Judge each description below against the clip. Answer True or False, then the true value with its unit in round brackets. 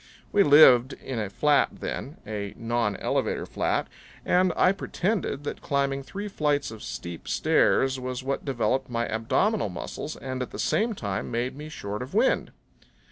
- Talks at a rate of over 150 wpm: True (160 wpm)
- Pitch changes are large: False (4.7 semitones)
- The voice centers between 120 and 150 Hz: True (135 Hz)